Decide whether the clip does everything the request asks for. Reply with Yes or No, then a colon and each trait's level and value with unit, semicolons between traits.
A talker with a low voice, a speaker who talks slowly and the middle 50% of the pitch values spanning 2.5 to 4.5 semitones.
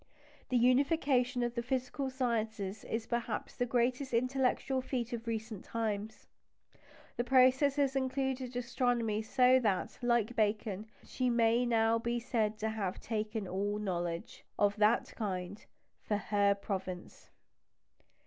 No: high, 235 Hz; slow, 130 wpm; average, 3.1 semitones